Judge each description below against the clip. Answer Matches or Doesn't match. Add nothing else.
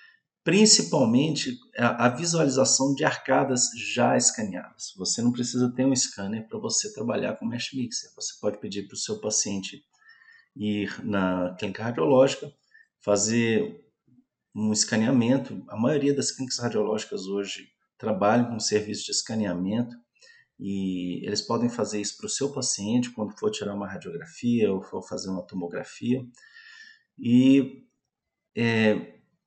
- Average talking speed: Matches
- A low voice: Matches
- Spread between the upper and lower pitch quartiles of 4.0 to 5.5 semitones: Matches